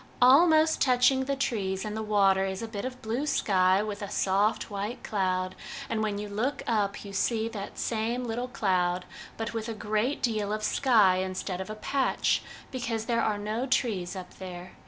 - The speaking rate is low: No, average, 190 wpm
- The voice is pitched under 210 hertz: No, high, 215 Hz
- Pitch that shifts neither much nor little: Yes, average, 3.8 semitones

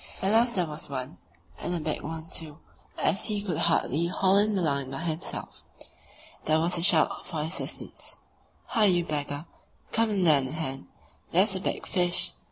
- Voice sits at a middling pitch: Yes, medium, 165 Hz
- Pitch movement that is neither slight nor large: Yes, average, 3.9 semitones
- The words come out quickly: No, average, 180 wpm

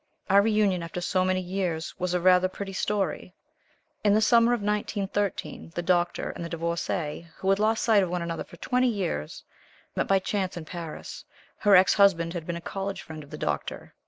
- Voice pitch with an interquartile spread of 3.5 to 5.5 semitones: No, average, 2.9 semitones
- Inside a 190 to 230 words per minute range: Yes, average, 200 wpm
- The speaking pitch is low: No, medium, 185 Hz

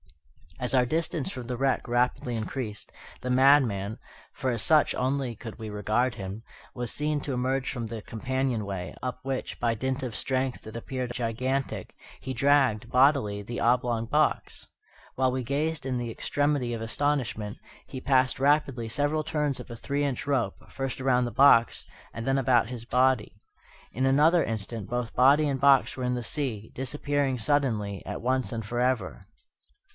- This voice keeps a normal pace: Yes, average, 170 wpm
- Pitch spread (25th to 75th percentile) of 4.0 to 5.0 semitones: No, average, 2.9 semitones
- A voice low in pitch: Yes, low, 125 Hz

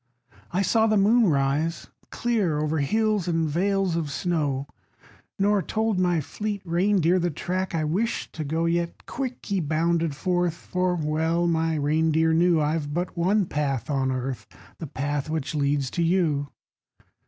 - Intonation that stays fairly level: No, average, 3.5 semitones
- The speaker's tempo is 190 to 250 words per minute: No, average, 155 wpm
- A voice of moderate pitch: Yes, medium, 165 Hz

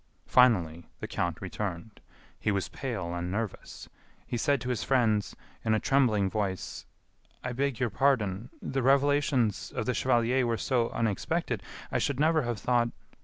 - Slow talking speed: No, average, 155 wpm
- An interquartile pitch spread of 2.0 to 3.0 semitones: No, average, 4.3 semitones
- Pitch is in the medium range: No, low, 115 Hz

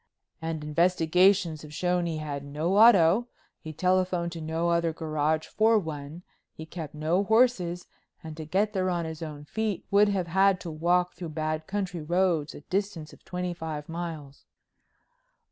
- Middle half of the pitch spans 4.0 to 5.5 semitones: No, average, 2.9 semitones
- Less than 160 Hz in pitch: No, medium, 170 Hz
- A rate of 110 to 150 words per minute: No, average, 165 wpm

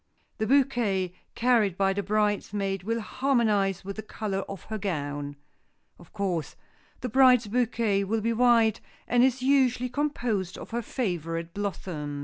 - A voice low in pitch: No, high, 210 Hz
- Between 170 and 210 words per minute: No, average, 145 wpm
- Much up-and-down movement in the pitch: No, average, 4.0 semitones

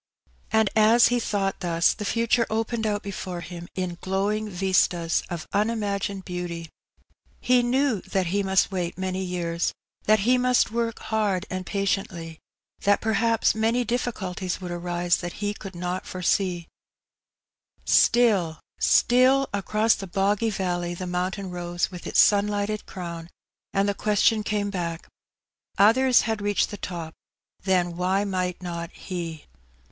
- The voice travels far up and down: No, average, 3.4 semitones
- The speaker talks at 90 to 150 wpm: Yes, average, 145 wpm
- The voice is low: No, high, 195 Hz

